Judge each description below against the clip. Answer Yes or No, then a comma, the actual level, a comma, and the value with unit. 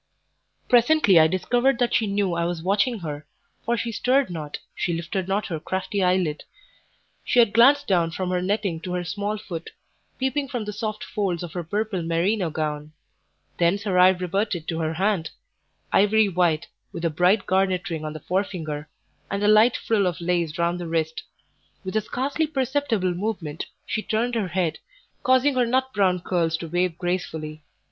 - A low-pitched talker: No, medium, 185 Hz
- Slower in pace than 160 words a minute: No, average, 180 wpm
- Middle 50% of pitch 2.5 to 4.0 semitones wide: No, average, 4.4 semitones